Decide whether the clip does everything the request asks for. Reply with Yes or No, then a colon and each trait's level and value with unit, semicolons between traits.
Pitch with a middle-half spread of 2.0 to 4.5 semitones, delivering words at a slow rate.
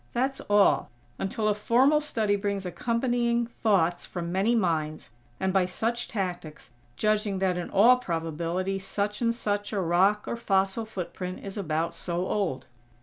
No: average, 4.0 semitones; average, 150 wpm